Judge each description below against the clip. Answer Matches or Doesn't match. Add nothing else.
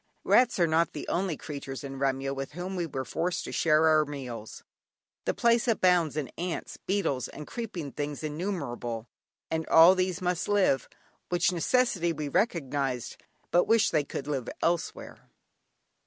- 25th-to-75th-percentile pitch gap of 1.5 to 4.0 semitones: Doesn't match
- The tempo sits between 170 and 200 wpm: Doesn't match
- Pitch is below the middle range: Doesn't match